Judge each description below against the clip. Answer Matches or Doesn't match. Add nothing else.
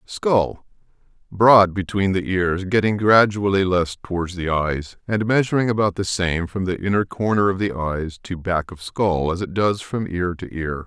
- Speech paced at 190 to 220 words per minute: Doesn't match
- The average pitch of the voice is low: Matches